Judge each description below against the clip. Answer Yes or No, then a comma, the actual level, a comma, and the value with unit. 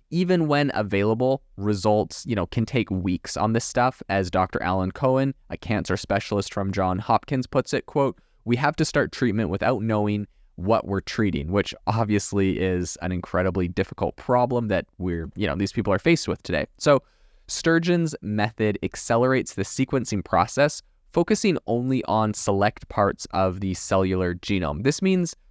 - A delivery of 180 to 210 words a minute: No, average, 165 wpm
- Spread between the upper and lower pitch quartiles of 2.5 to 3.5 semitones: No, wide, 5.5 semitones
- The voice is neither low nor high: No, low, 105 Hz